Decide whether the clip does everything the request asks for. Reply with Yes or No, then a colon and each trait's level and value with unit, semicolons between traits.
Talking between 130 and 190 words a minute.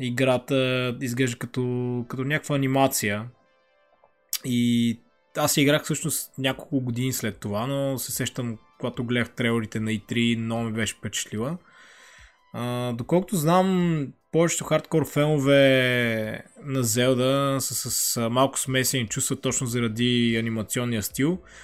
No: average, 120 wpm